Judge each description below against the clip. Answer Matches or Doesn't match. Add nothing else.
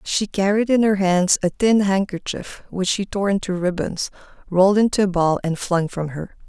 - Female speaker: Matches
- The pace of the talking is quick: Doesn't match